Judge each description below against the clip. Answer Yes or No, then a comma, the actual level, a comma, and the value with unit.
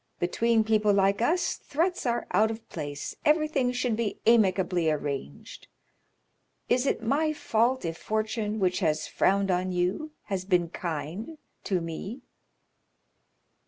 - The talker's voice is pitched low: No, high, 210 Hz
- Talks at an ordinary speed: No, slow, 130 wpm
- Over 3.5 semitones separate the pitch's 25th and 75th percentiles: Yes, average, 5.0 semitones